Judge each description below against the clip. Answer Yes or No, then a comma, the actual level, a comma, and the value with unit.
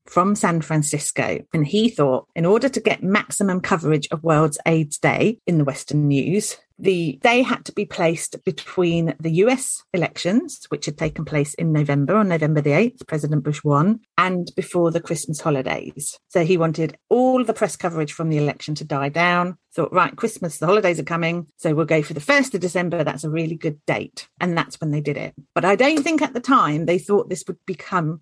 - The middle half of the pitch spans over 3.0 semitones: Yes, average, 4.0 semitones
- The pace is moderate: No, fast, 210 wpm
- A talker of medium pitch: Yes, medium, 165 Hz